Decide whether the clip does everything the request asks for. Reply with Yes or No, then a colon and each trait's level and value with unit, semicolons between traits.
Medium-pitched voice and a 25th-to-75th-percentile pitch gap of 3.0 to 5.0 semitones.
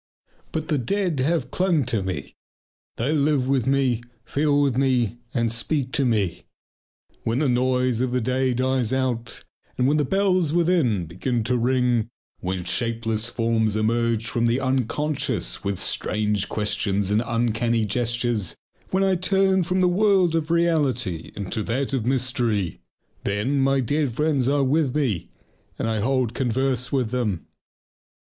No: low, 125 Hz; average, 3.9 semitones